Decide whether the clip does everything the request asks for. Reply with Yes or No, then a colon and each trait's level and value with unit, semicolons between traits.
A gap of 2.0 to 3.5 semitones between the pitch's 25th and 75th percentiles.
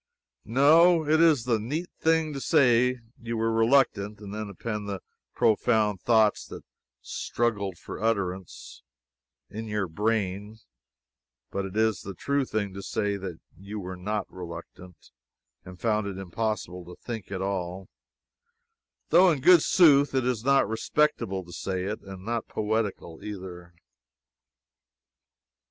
No: average, 4.1 semitones